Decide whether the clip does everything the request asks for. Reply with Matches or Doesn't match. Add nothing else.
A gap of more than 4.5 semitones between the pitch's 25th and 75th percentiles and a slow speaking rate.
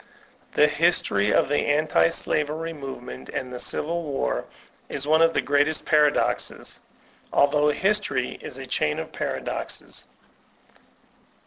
Doesn't match